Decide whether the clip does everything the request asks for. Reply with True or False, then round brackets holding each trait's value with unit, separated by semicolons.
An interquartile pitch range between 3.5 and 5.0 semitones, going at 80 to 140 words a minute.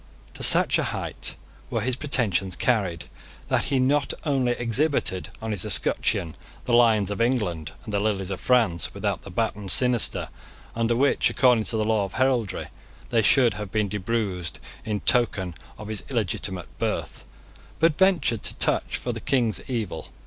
False (4.0 semitones; 165 wpm)